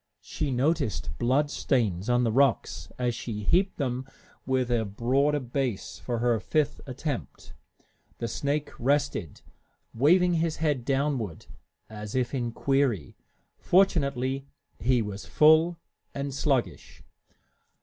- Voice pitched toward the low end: Yes, low, 130 Hz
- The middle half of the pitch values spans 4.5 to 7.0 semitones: No, average, 3.6 semitones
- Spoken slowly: Yes, slow, 120 wpm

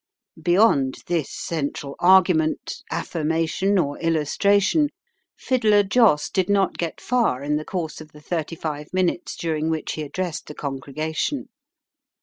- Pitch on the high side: No, medium, 165 Hz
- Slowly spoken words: Yes, slow, 130 wpm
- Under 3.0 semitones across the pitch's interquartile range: No, average, 4.0 semitones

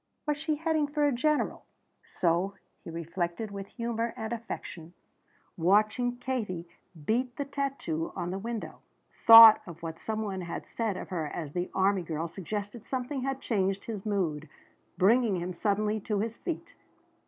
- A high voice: Yes, high, 210 Hz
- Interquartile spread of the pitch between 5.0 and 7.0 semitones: Yes, wide, 5.4 semitones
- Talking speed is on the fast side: No, average, 160 wpm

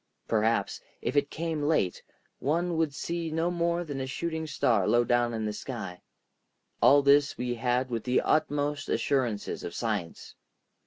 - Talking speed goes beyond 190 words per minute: No, average, 160 wpm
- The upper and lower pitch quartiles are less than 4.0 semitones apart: No, average, 5.2 semitones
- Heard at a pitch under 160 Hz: Yes, medium, 140 Hz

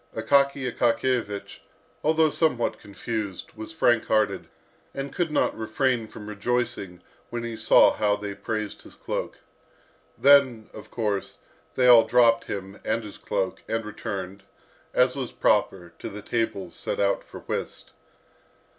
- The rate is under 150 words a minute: Yes, average, 140 wpm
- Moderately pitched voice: No, low, 110 Hz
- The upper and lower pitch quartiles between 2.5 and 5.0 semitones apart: Yes, average, 3.5 semitones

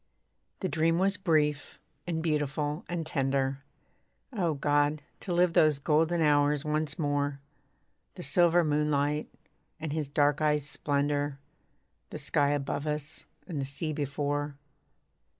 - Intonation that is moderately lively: No, narrow, 1.8 semitones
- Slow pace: Yes, slow, 130 wpm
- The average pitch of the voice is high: No, medium, 150 Hz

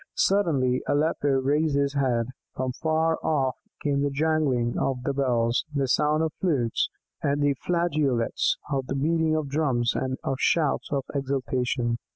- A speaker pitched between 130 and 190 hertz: Yes, medium, 140 Hz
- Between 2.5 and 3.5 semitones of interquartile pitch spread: Yes, average, 3.0 semitones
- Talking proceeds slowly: No, average, 150 wpm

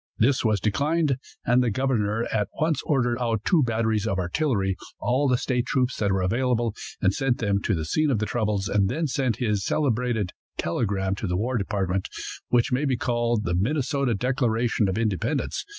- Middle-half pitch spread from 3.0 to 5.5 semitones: Yes, average, 4.1 semitones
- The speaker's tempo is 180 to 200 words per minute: Yes, average, 185 wpm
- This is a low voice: Yes, low, 115 Hz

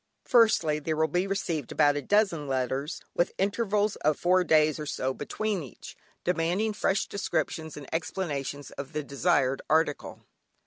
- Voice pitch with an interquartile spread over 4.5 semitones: Yes, average, 4.9 semitones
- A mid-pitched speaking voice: Yes, medium, 160 Hz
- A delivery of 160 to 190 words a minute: No, average, 150 wpm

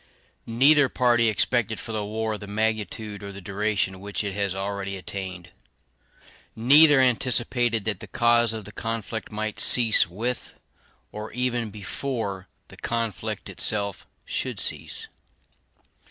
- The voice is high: No, low, 110 Hz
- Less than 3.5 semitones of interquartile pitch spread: Yes, average, 2.7 semitones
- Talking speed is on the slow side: Yes, slow, 130 wpm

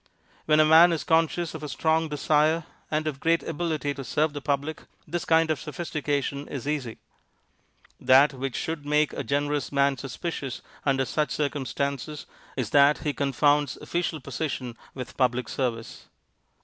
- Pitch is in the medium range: Yes, medium, 145 Hz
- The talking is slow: No, average, 155 wpm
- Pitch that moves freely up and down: No, narrow, 2.4 semitones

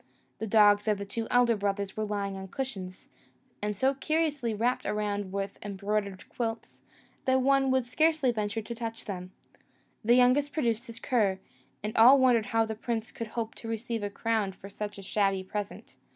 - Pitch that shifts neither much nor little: Yes, average, 3.2 semitones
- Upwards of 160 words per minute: Yes, average, 180 wpm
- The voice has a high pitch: Yes, high, 220 Hz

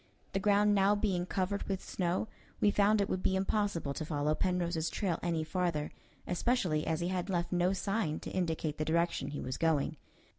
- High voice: No, medium, 180 Hz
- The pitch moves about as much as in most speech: Yes, average, 3.5 semitones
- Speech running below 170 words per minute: No, average, 190 wpm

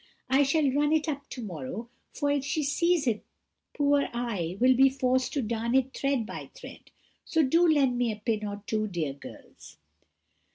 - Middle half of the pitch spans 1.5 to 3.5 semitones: No, average, 4.7 semitones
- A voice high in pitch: Yes, very high, 260 Hz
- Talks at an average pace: Yes, average, 190 wpm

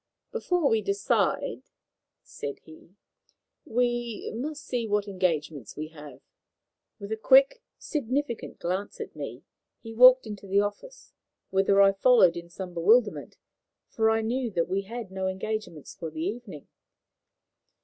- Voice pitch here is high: Yes, high, 205 Hz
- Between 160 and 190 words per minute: No, average, 140 wpm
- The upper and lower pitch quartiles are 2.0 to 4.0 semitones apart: No, average, 4.7 semitones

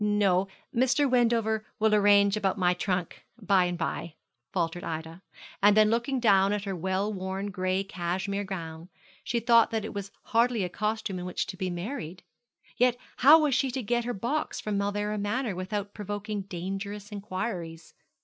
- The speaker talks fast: No, average, 170 wpm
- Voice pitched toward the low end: No, high, 200 Hz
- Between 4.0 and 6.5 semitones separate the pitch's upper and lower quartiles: No, average, 2.9 semitones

